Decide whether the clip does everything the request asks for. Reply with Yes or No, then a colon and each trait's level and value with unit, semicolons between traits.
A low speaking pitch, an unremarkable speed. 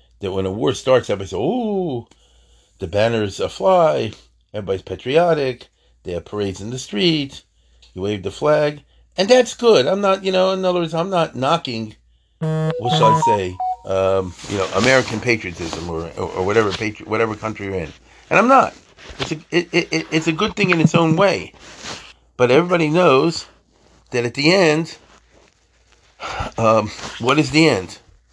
Yes: low, 130 Hz; average, 175 wpm